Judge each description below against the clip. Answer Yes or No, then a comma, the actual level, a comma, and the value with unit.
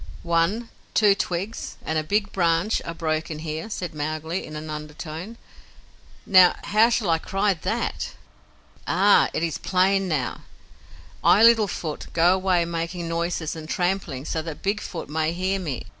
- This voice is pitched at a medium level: Yes, medium, 170 Hz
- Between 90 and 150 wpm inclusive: No, average, 160 wpm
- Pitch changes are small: No, average, 3.5 semitones